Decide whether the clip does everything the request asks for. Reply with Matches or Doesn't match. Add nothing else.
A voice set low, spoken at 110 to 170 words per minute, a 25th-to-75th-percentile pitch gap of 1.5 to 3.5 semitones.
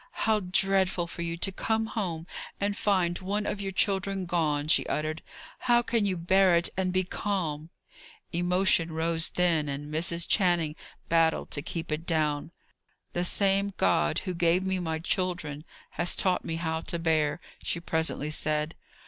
Doesn't match